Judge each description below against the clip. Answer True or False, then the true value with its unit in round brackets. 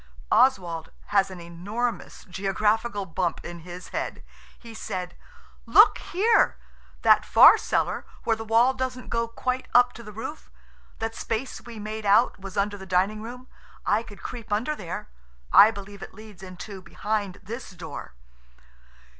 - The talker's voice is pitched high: True (210 Hz)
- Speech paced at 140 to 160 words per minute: True (145 wpm)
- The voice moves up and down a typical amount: True (3.4 semitones)